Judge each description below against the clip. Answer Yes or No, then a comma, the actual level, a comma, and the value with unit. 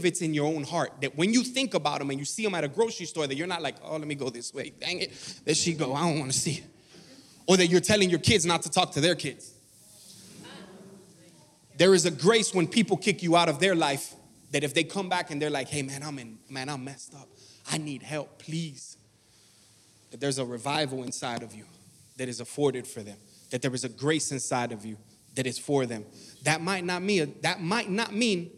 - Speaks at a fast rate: Yes, fast, 245 wpm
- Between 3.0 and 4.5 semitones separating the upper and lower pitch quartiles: No, average, 5.3 semitones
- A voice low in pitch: No, medium, 150 Hz